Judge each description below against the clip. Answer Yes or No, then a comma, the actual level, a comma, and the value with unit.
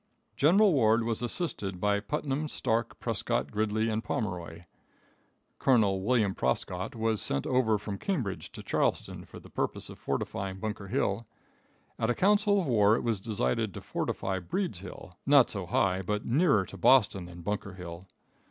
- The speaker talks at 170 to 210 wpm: No, average, 160 wpm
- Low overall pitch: Yes, low, 105 Hz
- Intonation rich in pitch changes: No, average, 4.3 semitones